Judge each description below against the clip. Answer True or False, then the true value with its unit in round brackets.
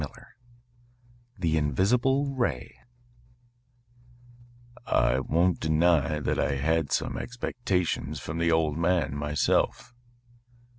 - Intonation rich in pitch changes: False (3.8 semitones)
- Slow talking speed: True (95 wpm)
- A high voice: False (80 Hz)